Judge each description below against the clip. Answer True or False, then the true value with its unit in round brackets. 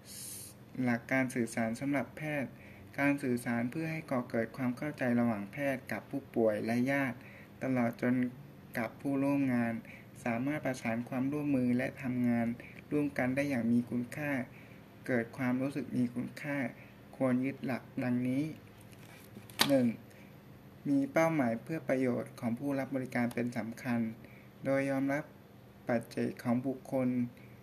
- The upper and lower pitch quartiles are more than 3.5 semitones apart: False (2.9 semitones)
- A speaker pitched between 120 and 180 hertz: True (125 Hz)